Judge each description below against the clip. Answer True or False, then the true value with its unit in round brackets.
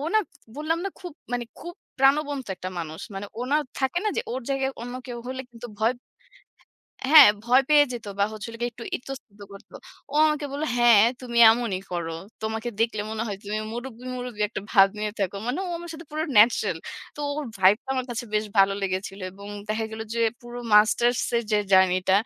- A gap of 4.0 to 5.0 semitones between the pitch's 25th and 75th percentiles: True (4.4 semitones)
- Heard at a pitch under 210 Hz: False (235 Hz)